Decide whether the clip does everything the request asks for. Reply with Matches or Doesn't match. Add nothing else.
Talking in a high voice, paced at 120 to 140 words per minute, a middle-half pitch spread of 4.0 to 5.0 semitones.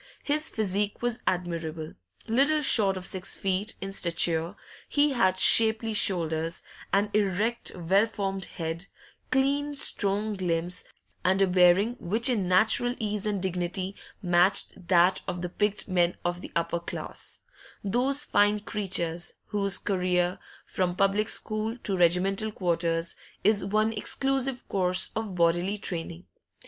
Doesn't match